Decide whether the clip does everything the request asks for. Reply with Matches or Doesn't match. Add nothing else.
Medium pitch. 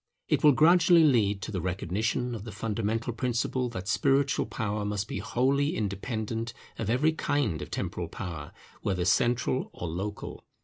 Doesn't match